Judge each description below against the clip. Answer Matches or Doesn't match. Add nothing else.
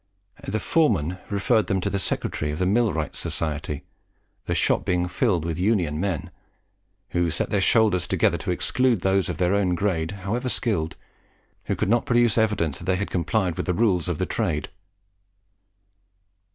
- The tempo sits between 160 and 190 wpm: Matches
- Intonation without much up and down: Doesn't match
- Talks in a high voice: Doesn't match